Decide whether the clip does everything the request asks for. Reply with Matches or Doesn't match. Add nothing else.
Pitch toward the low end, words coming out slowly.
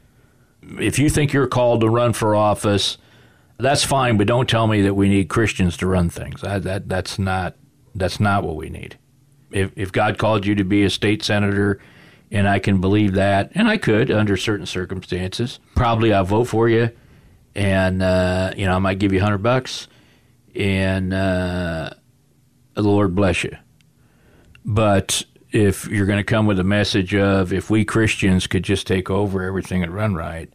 Doesn't match